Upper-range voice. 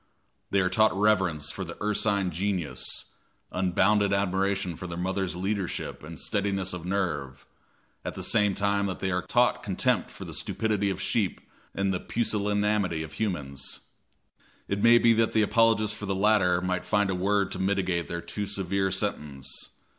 No: very low, 95 Hz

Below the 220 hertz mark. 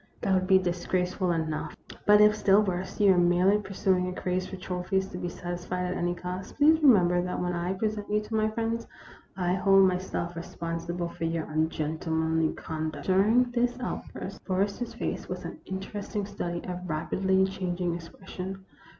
Yes: medium, 185 Hz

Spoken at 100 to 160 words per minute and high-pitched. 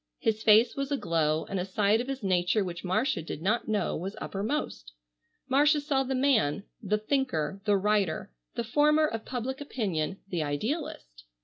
No: average, 170 wpm; high, 210 Hz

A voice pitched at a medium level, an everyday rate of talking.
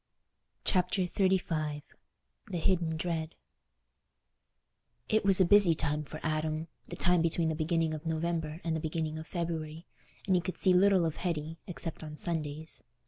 Yes: medium, 165 Hz; average, 150 wpm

